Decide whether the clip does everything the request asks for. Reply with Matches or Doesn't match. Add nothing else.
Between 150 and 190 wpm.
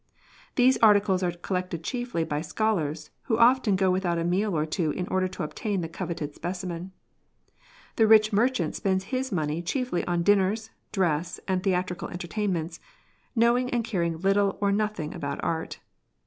Matches